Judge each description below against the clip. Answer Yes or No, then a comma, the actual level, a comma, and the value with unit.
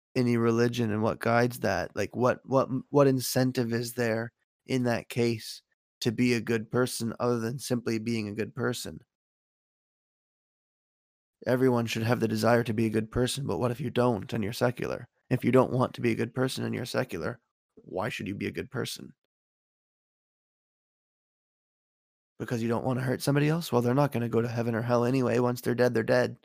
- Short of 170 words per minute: No, average, 200 wpm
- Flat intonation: Yes, narrow, 1.6 semitones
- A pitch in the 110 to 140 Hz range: Yes, low, 120 Hz